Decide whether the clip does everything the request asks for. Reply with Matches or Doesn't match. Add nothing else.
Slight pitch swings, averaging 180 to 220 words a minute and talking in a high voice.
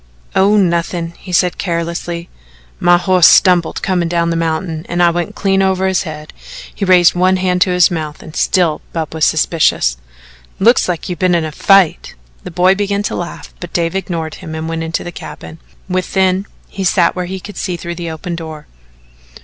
Doesn't match